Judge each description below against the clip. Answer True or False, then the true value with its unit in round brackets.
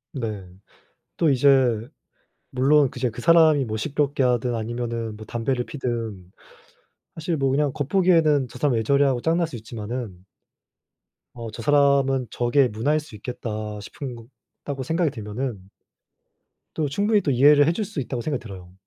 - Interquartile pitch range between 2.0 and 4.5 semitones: True (4.2 semitones)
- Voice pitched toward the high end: False (130 Hz)